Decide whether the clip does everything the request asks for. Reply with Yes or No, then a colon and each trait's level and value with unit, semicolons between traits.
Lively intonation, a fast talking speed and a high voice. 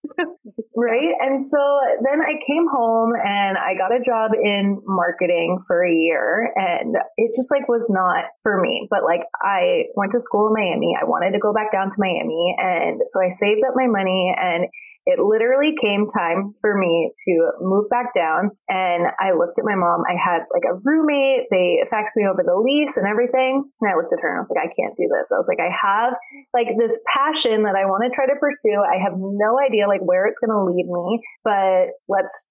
Yes: wide, 6.0 semitones; fast, 220 wpm; high, 220 Hz